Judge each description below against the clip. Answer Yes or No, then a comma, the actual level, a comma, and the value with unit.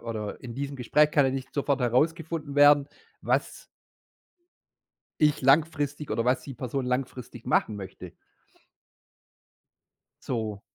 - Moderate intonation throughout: Yes, average, 3.1 semitones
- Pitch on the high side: No, low, 135 Hz